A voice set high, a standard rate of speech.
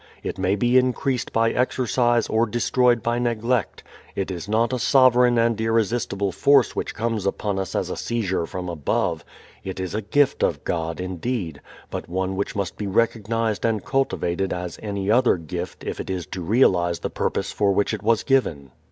No: low, 110 Hz; average, 185 wpm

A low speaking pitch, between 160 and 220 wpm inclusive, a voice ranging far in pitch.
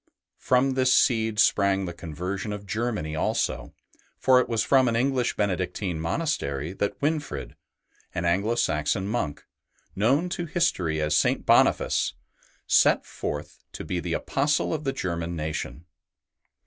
No: low, 100 Hz; average, 140 wpm; wide, 7.1 semitones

